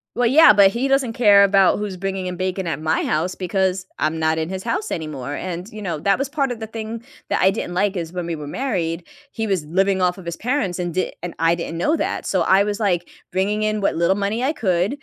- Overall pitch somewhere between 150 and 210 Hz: Yes, high, 190 Hz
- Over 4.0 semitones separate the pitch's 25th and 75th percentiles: No, average, 3.6 semitones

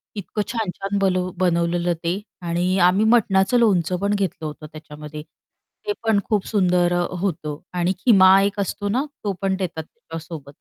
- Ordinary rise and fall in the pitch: Yes, average, 3.0 semitones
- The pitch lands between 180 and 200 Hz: Yes, medium, 185 Hz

